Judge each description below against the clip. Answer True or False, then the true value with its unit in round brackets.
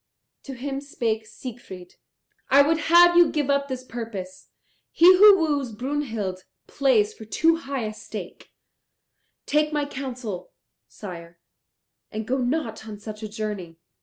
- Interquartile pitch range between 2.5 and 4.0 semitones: False (5.3 semitones)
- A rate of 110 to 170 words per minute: True (140 wpm)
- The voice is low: False (250 Hz)